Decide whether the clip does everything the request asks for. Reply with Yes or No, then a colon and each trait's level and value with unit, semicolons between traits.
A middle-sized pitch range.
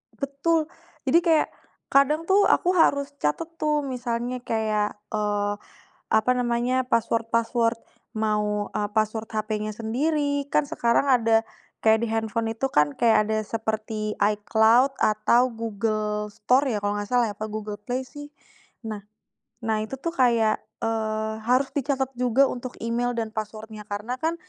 Yes: average, 3.2 semitones